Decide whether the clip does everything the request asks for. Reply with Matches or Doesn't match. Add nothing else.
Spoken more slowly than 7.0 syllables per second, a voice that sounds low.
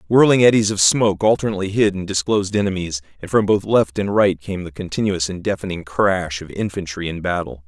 Matches